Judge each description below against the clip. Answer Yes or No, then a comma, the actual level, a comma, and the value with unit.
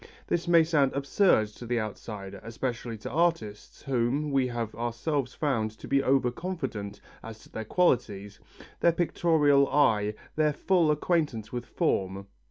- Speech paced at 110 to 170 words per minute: Yes, average, 150 wpm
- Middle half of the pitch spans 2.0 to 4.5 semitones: No, wide, 5.6 semitones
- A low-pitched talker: Yes, low, 125 Hz